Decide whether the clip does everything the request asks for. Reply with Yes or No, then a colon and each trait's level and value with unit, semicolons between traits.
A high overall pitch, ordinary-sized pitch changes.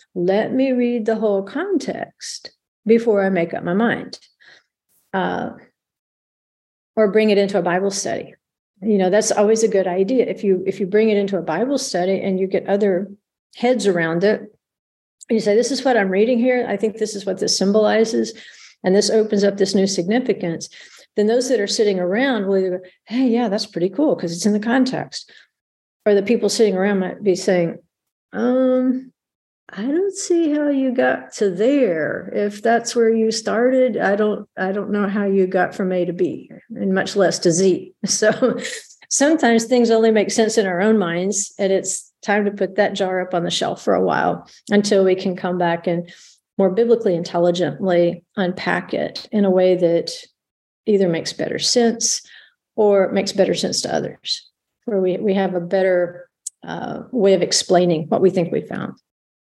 Yes: high, 205 Hz; average, 3.6 semitones